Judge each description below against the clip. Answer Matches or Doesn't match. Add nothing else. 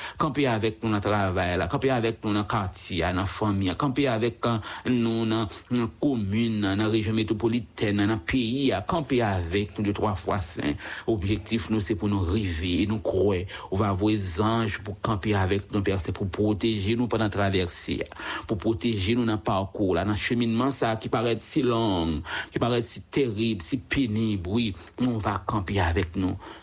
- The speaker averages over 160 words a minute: Matches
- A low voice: Matches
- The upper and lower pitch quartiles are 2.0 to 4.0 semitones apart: Matches